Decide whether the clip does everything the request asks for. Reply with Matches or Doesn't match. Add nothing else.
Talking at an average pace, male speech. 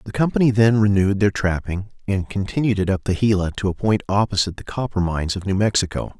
Doesn't match